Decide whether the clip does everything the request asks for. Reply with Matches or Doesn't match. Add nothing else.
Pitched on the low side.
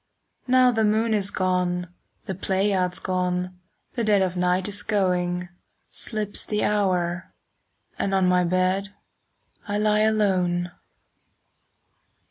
Doesn't match